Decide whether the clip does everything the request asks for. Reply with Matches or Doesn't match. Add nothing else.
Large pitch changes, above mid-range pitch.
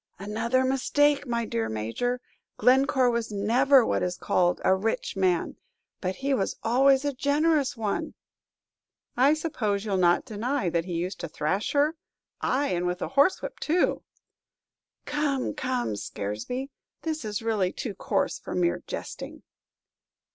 Matches